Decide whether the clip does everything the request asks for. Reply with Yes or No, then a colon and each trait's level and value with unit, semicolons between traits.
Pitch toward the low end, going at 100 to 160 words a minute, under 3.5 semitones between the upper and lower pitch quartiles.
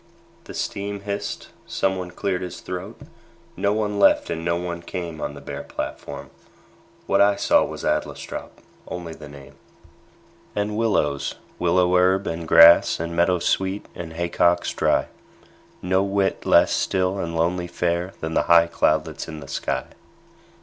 Yes: very low, 90 Hz; average, 150 wpm; narrow, 2.4 semitones